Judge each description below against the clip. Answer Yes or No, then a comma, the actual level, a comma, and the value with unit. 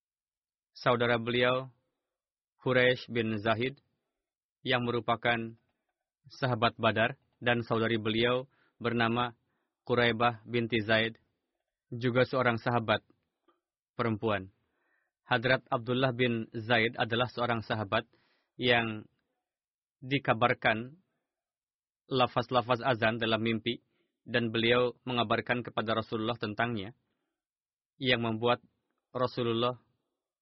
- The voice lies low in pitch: Yes, low, 120 Hz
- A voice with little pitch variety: Yes, narrow, 1.5 semitones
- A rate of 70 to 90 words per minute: Yes, slow, 85 wpm